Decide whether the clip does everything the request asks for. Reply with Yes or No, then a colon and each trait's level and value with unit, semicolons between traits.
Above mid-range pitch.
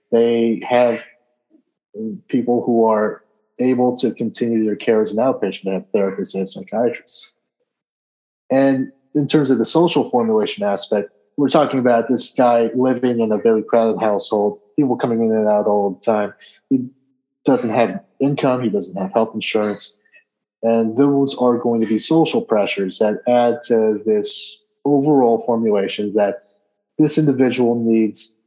No: low, 115 Hz